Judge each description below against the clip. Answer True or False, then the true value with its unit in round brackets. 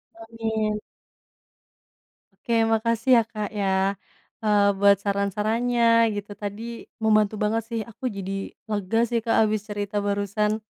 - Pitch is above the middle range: True (215 Hz)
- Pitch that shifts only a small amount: True (1.9 semitones)